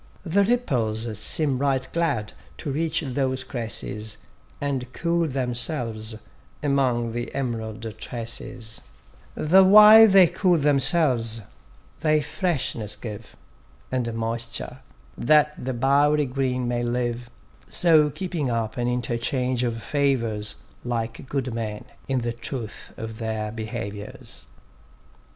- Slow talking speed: Yes, slow, 115 wpm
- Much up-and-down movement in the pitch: No, average, 4.2 semitones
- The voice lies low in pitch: Yes, low, 125 Hz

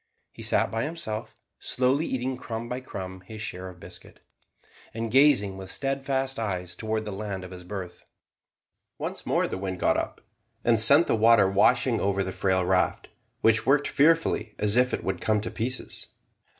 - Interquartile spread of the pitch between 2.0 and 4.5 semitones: No, average, 5.0 semitones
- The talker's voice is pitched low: Yes, low, 110 Hz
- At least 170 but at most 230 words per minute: Yes, average, 175 wpm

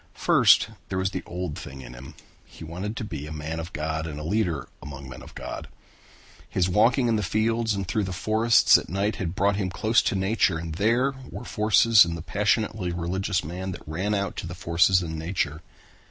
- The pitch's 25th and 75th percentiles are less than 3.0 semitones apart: No, average, 4.6 semitones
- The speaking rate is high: Yes, fast, 210 wpm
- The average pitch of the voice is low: Yes, very low, 90 Hz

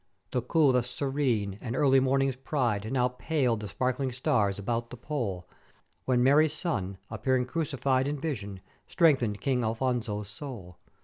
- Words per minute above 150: No, average, 140 wpm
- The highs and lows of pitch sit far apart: No, average, 4.0 semitones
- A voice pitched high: No, low, 125 Hz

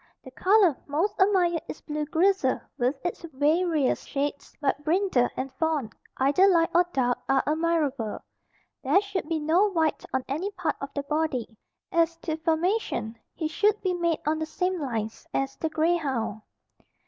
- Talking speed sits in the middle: Yes, average, 165 wpm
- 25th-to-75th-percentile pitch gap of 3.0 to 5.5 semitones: Yes, average, 4.2 semitones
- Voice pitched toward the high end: Yes, very high, 315 Hz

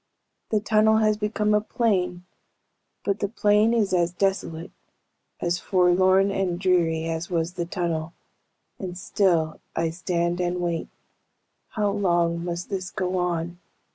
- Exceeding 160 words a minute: No, average, 140 wpm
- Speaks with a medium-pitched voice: Yes, medium, 180 Hz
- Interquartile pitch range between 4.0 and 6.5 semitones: No, average, 2.7 semitones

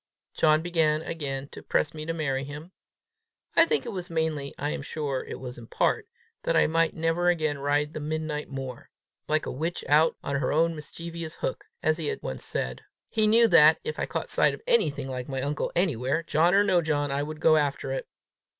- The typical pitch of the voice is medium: Yes, medium, 155 Hz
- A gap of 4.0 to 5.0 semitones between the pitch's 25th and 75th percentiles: No, average, 2.7 semitones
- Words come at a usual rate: No, fast, 215 wpm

